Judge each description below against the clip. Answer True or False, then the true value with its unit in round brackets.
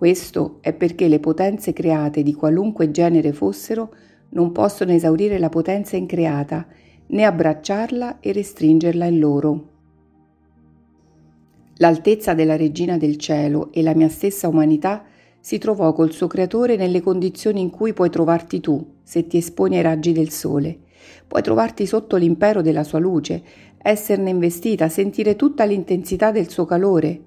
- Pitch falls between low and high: True (170 Hz)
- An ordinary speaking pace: True (145 wpm)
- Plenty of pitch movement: False (3.9 semitones)